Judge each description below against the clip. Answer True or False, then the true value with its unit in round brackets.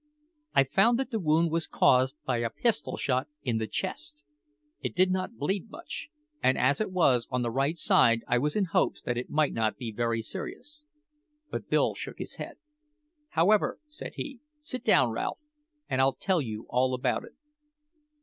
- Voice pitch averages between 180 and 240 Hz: False (145 Hz)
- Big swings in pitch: True (7.6 semitones)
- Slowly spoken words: False (185 wpm)